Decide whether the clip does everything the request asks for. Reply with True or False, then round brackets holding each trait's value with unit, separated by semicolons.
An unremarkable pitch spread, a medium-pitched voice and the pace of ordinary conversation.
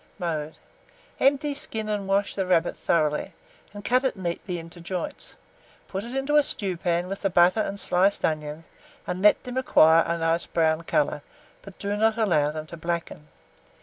True (4.1 semitones; 180 Hz; 175 wpm)